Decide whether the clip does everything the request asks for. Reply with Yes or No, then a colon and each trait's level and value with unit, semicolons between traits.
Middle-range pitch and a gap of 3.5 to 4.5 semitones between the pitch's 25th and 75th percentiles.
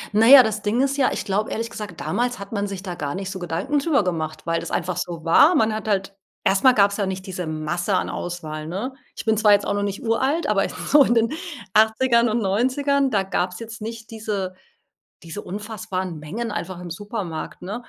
No: high, 205 Hz; average, 3.9 semitones